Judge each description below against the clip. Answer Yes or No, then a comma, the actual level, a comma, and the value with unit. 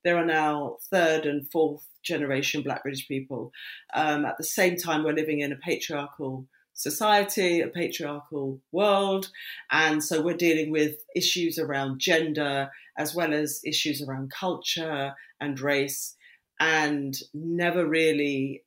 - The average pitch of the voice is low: No, medium, 155 Hz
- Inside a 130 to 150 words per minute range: Yes, average, 140 wpm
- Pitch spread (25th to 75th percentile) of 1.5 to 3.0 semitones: Yes, average, 2.7 semitones